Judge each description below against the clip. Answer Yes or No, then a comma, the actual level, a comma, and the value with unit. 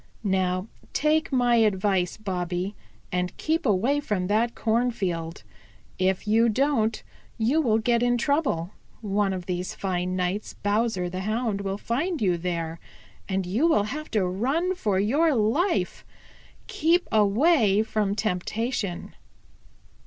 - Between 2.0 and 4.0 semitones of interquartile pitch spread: No, average, 4.8 semitones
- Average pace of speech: No, slow, 130 wpm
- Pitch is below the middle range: No, high, 215 Hz